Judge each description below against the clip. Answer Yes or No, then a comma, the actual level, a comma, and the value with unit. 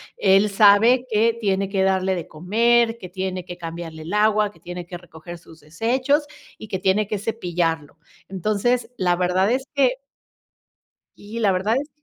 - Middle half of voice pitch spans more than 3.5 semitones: Yes, average, 4.0 semitones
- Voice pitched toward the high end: Yes, high, 195 Hz